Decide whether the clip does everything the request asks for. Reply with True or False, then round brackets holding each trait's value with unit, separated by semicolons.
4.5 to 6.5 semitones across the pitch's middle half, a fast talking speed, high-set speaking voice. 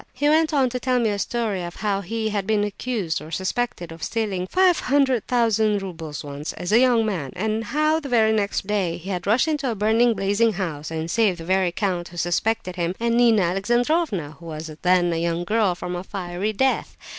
True (5.0 semitones; 215 wpm; 205 Hz)